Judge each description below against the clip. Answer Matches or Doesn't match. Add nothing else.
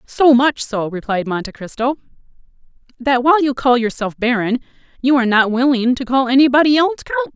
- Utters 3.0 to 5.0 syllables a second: Doesn't match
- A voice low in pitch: Doesn't match